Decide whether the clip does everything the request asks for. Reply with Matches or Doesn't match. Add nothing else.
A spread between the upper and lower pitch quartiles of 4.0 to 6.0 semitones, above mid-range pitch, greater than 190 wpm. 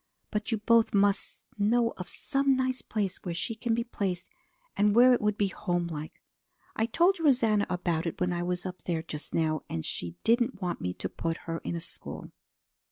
Matches